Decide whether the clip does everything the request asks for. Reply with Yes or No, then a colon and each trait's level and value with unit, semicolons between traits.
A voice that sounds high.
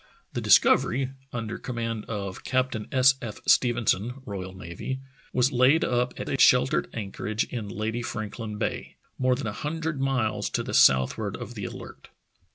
No: low, 120 Hz